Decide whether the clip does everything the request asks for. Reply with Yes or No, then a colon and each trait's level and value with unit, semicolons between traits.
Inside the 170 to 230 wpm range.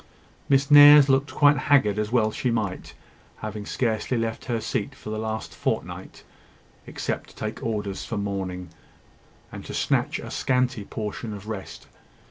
No: average, 155 wpm